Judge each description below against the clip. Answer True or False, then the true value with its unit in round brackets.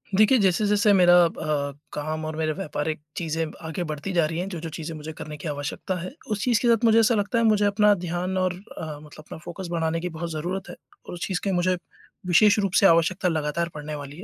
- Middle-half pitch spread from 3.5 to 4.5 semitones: True (3.9 semitones)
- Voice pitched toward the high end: False (170 Hz)